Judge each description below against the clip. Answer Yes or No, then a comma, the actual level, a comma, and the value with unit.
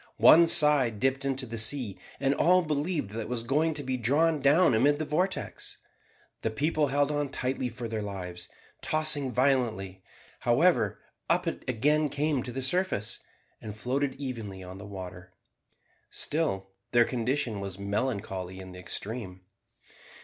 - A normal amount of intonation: No, wide, 6.0 semitones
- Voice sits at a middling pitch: No, low, 130 Hz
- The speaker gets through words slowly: No, average, 155 wpm